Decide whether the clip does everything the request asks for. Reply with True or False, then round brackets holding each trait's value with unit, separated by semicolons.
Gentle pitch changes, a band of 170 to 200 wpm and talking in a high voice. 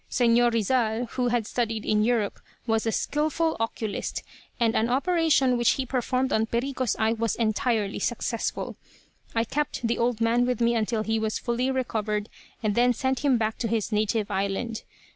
True (2.3 semitones; 175 wpm; 235 Hz)